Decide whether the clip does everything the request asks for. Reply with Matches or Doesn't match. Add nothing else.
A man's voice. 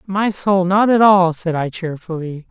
Matches